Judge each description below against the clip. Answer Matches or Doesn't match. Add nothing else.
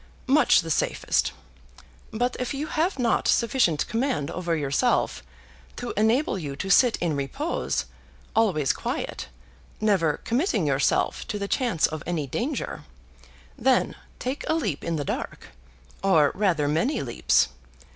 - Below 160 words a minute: Matches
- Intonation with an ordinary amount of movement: Doesn't match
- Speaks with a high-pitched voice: Matches